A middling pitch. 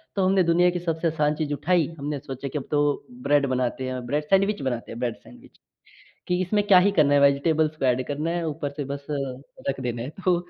Yes: medium, 150 Hz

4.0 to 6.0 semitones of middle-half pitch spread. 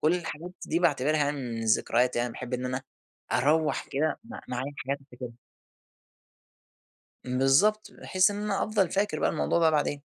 Yes: average, 5.2 semitones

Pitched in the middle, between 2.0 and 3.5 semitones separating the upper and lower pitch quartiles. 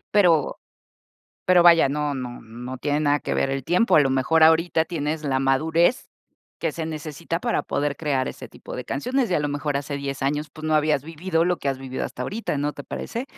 Yes: medium, 150 Hz; average, 3.1 semitones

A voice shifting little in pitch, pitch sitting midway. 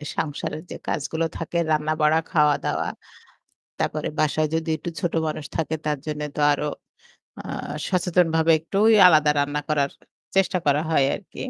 Yes: narrow, 1.6 semitones; medium, 155 Hz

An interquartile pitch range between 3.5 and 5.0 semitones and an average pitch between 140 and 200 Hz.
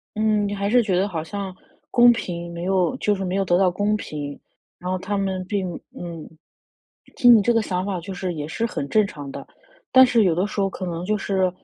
No: average, 2.7 semitones; high, 190 Hz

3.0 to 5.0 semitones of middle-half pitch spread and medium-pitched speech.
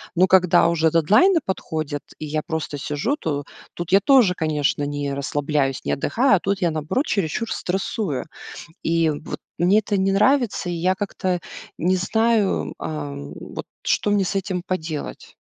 Yes: average, 4.7 semitones; medium, 175 Hz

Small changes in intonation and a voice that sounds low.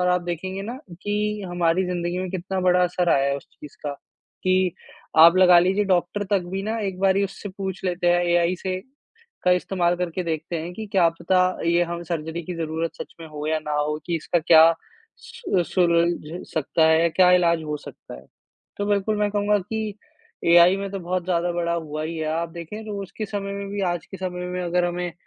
No: narrow, 2.2 semitones; medium, 180 Hz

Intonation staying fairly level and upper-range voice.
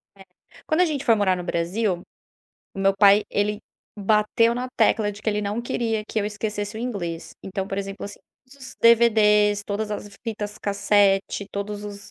Yes: narrow, 1.8 semitones; high, 210 Hz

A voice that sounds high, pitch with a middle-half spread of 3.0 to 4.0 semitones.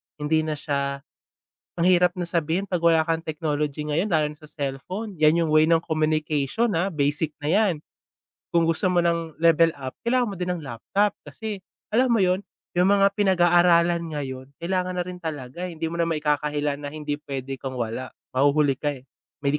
No: medium, 160 Hz; average, 3.3 semitones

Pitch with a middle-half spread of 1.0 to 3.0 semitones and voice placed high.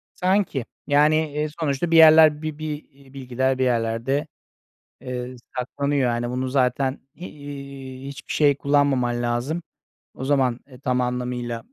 No: narrow, 2.6 semitones; low, 135 Hz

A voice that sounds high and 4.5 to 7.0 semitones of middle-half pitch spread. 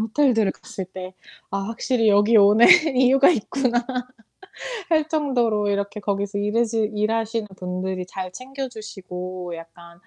No: high, 210 Hz; average, 3.9 semitones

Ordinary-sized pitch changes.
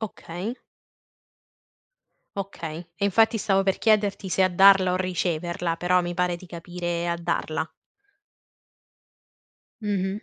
No: narrow, 2.2 semitones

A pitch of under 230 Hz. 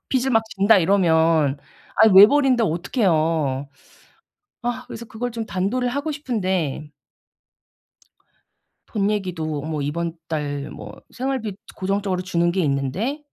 Yes: high, 190 Hz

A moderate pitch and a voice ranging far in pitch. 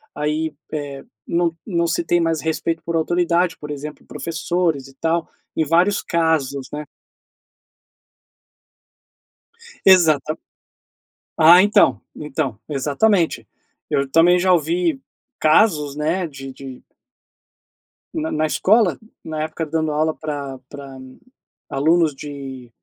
No: medium, 160 Hz; average, 2.8 semitones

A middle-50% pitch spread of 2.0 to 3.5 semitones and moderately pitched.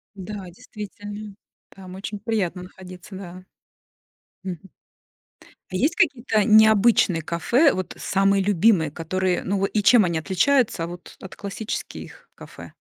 No: average, 2.8 semitones; high, 195 Hz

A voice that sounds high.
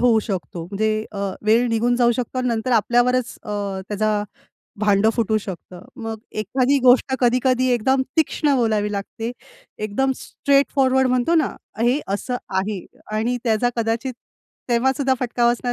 Yes: high, 235 Hz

